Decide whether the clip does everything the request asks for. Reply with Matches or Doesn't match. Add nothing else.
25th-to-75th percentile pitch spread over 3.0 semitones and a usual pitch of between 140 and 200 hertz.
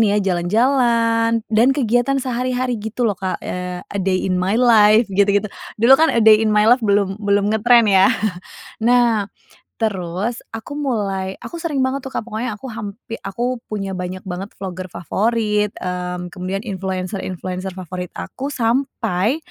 Doesn't match